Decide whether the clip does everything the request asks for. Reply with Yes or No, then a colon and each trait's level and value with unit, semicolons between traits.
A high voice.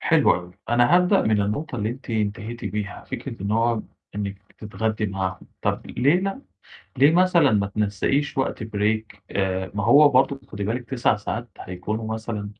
No: low, 110 Hz